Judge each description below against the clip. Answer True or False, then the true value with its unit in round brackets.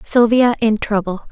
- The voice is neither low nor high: False (220 Hz)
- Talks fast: False (135 wpm)